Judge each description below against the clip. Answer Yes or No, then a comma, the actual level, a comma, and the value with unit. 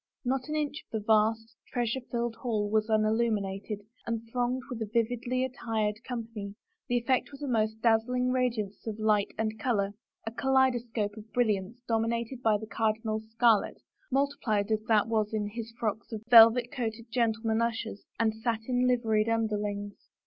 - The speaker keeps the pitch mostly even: Yes, narrow, 2.1 semitones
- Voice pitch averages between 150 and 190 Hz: No, high, 225 Hz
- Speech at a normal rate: Yes, average, 170 wpm